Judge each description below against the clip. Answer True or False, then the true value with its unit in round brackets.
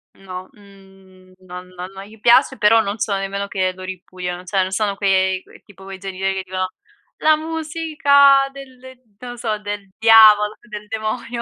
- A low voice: False (200 Hz)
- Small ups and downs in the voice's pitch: False (3.2 semitones)